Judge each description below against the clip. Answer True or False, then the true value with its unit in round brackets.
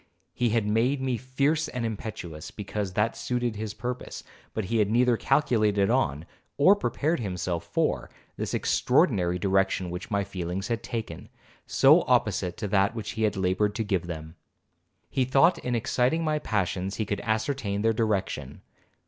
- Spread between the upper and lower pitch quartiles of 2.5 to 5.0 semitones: True (4.2 semitones)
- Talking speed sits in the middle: True (165 wpm)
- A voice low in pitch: True (110 Hz)